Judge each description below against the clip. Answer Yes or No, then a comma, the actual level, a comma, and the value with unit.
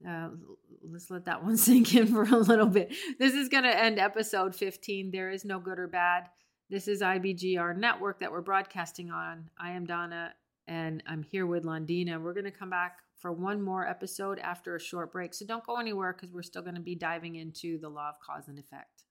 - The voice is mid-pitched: Yes, medium, 180 Hz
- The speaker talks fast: Yes, fast, 225 wpm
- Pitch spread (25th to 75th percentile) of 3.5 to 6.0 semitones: No, average, 2.8 semitones